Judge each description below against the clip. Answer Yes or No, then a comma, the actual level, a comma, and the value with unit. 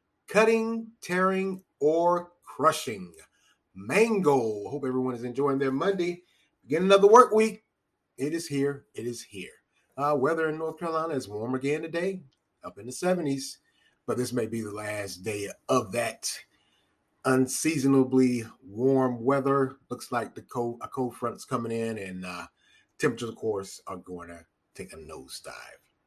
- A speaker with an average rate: Yes, average, 150 wpm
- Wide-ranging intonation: Yes, wide, 6.4 semitones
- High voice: No, low, 135 Hz